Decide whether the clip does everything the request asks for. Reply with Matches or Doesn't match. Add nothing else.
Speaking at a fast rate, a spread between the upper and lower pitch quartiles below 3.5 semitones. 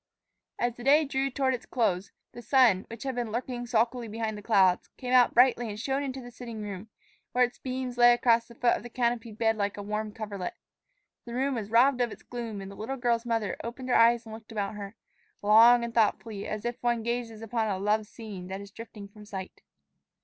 Matches